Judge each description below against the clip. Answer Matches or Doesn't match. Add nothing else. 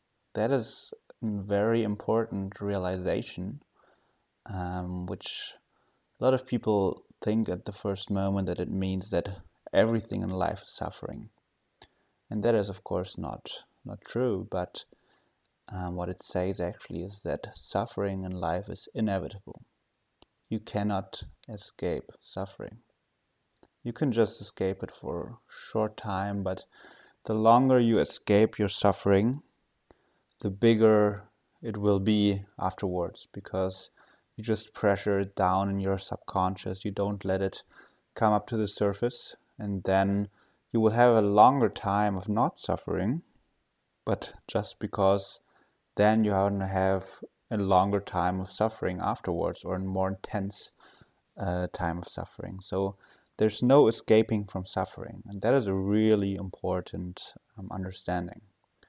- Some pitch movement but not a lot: Doesn't match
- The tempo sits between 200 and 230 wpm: Doesn't match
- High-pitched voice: Doesn't match